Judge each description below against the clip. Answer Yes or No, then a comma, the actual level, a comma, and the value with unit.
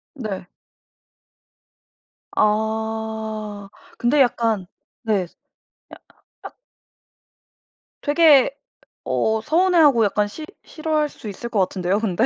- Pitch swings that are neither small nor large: Yes, average, 5.0 semitones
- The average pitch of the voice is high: Yes, high, 220 Hz